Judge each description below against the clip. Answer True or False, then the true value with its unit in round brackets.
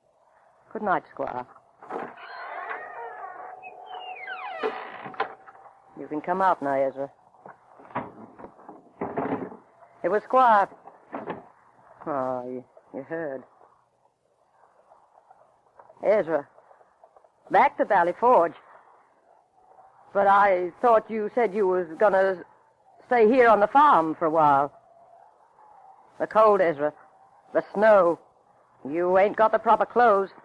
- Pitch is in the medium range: False (200 Hz)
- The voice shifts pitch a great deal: True (7.2 semitones)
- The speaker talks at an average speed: False (95 wpm)